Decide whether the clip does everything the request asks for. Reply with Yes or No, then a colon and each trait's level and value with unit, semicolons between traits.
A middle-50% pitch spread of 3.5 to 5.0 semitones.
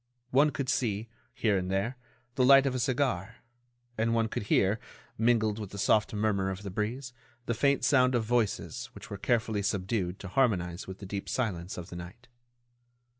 Yes: average, 4.0 semitones